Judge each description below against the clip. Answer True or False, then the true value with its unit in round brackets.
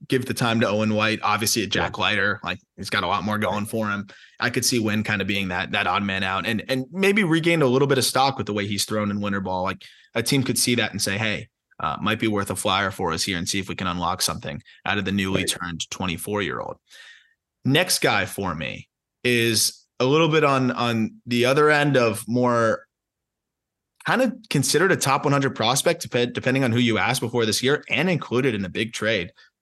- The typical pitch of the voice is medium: False (115 Hz)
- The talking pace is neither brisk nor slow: False (235 wpm)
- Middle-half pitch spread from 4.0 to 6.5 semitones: True (4.4 semitones)